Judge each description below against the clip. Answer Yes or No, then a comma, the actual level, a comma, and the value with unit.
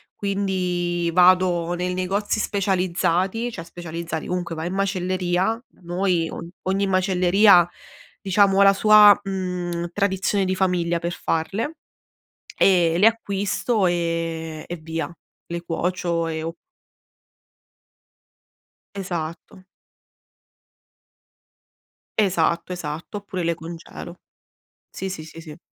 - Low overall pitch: No, medium, 180 Hz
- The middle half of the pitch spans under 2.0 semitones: No, narrow, 2.4 semitones